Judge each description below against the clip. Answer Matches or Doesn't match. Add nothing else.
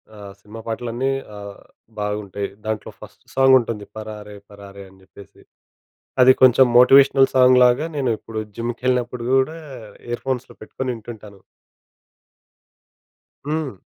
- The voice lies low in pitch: Matches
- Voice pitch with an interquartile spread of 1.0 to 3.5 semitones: Doesn't match